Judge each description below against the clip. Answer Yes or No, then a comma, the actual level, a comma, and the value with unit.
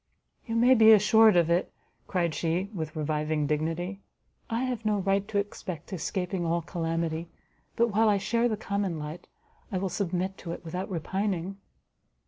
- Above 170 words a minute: No, average, 165 wpm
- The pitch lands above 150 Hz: Yes, medium, 185 Hz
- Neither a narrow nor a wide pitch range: Yes, average, 3.8 semitones